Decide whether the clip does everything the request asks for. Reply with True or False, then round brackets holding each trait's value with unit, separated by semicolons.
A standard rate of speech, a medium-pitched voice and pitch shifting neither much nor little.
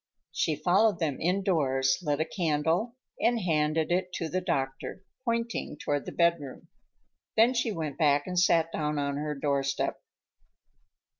True (145 wpm; 160 Hz; 4.0 semitones)